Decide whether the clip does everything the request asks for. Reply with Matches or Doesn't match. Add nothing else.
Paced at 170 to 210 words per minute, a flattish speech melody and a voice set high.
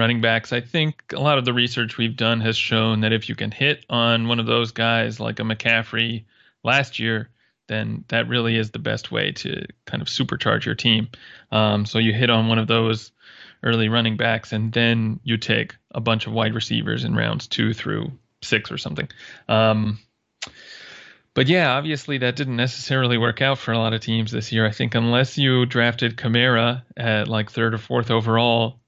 Doesn't match